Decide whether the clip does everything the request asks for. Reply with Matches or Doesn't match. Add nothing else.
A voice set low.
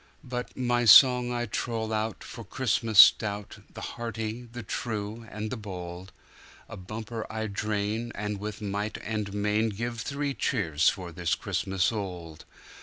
Matches